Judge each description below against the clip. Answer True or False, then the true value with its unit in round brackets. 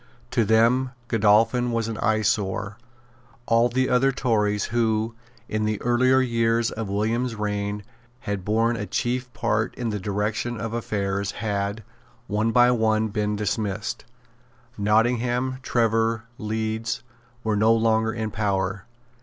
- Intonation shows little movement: True (2.1 semitones)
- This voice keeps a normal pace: False (130 wpm)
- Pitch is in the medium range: False (110 Hz)